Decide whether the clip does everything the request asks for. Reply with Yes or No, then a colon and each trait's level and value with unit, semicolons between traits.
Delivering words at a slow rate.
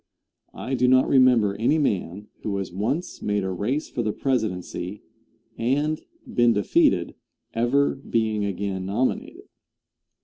Yes: slow, 130 wpm